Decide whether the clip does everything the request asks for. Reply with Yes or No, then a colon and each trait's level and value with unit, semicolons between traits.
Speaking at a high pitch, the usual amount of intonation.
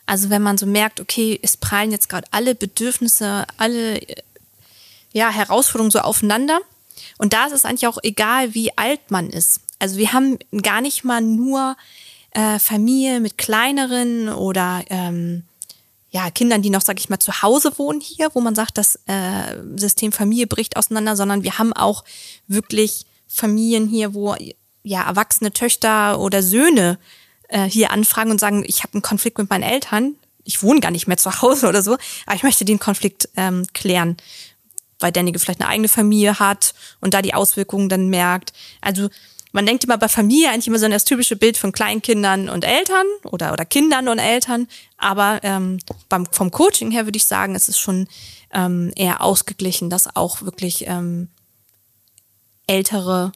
Yes: high, 210 Hz; average, 3.4 semitones